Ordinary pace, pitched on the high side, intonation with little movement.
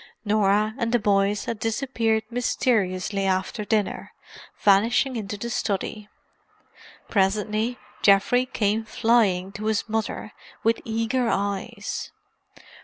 No: slow, 110 wpm; high, 215 Hz; narrow, 2.3 semitones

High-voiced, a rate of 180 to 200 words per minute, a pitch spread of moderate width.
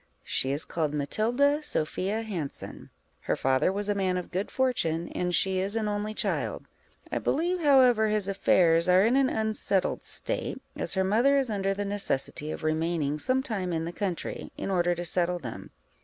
Yes: high, 195 Hz; average, 185 wpm; average, 4.4 semitones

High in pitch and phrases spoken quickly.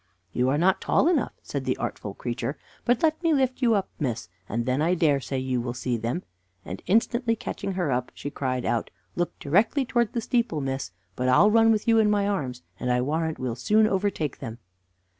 No: medium, 165 Hz; fast, 215 wpm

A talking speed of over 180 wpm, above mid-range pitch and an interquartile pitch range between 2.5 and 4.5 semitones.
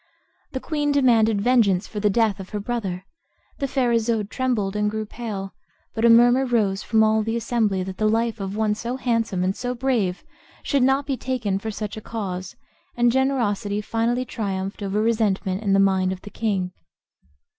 Yes: average, 190 wpm; high, 220 Hz; average, 3.4 semitones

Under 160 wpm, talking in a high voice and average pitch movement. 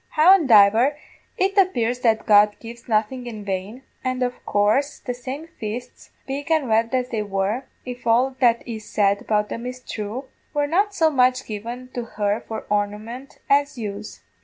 No: average, 170 wpm; high, 240 Hz; average, 3.7 semitones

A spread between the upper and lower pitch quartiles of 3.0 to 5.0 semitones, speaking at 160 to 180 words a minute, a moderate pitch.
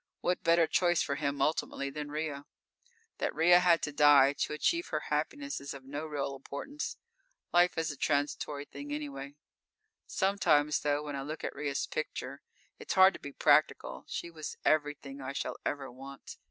No: narrow, 2.5 semitones; average, 175 wpm; medium, 145 Hz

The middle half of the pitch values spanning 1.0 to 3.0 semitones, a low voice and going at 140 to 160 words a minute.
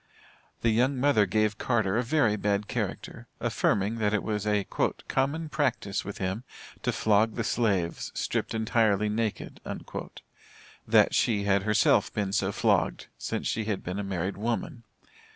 Yes: narrow, 2.4 semitones; low, 105 Hz; average, 150 wpm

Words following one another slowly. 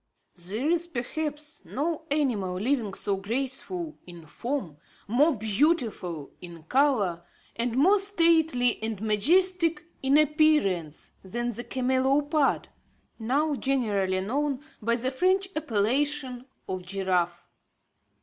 Yes: slow, 110 wpm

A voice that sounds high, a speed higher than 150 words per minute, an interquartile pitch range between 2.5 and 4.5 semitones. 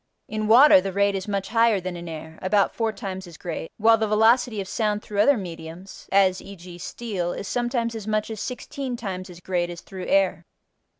Yes: high, 200 Hz; fast, 205 wpm; average, 3.4 semitones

